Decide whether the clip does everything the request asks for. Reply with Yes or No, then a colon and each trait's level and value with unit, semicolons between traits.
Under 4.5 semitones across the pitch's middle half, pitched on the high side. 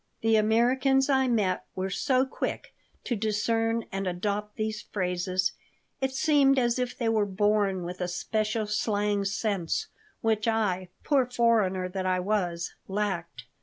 Yes: average, 3.6 semitones; high, 210 Hz